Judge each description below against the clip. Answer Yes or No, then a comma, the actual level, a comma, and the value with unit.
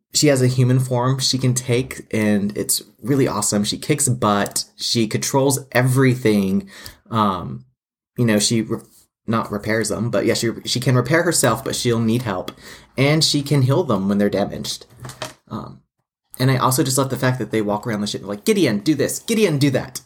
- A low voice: Yes, low, 120 Hz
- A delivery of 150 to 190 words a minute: No, average, 200 wpm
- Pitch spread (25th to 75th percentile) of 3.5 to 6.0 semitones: Yes, average, 4.2 semitones